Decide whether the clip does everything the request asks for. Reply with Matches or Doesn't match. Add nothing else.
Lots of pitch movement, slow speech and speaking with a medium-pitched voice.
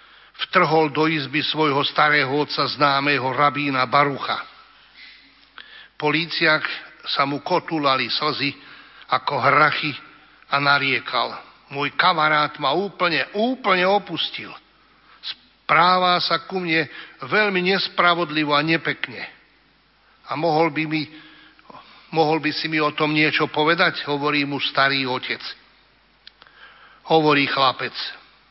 Doesn't match